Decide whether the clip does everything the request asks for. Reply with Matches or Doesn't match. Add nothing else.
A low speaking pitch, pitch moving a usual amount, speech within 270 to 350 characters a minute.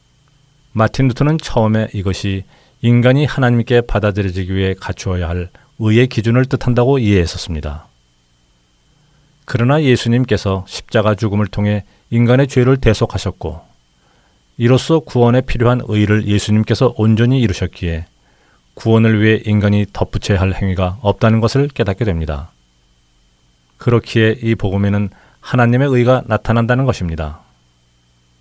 Matches